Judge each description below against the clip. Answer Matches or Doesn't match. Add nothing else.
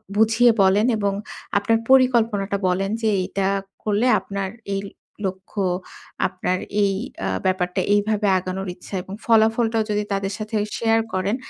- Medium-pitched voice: Doesn't match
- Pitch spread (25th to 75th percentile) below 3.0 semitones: Matches